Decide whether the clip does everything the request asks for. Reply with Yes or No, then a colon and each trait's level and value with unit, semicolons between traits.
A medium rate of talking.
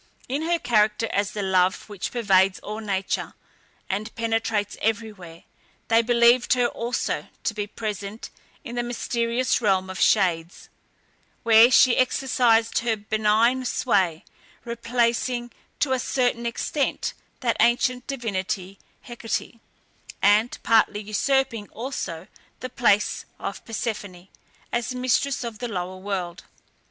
No: slow, 125 wpm